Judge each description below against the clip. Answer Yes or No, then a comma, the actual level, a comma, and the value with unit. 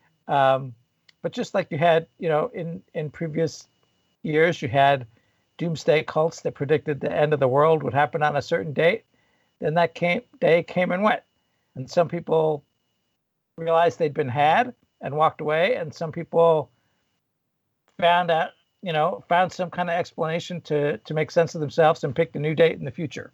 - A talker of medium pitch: Yes, medium, 160 Hz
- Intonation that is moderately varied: No, narrow, 2.3 semitones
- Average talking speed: Yes, average, 185 wpm